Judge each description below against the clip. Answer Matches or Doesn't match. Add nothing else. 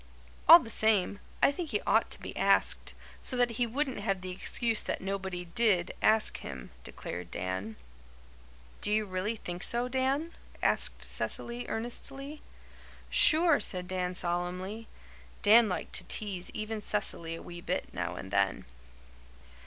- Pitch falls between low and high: Doesn't match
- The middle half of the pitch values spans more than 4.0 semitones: Matches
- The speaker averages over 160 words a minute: Doesn't match